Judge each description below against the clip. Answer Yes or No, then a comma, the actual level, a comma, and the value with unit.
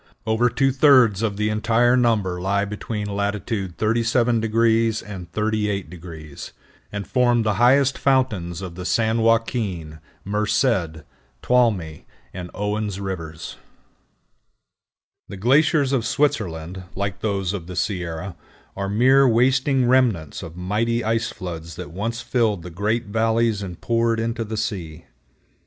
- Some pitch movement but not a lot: Yes, average, 4.0 semitones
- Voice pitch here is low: Yes, low, 105 Hz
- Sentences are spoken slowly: Yes, slow, 130 wpm